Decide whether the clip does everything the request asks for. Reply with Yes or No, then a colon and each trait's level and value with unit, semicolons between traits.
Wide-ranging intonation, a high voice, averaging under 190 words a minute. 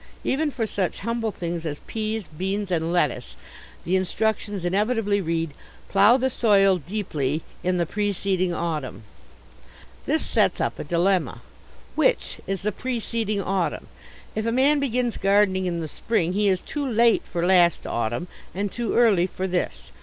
No: average, 4.1 semitones; high, 195 Hz; average, 155 wpm